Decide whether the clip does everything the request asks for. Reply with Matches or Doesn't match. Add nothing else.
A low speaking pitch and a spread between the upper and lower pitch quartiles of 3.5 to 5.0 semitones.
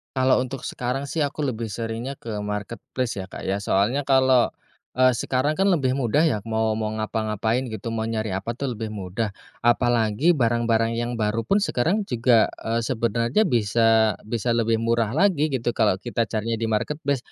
Doesn't match